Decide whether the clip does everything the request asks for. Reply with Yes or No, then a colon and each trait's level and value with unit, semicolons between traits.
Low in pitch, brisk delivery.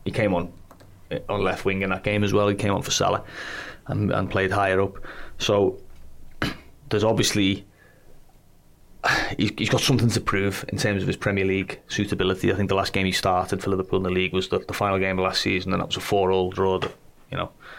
Yes: very low, 95 Hz; fast, 225 wpm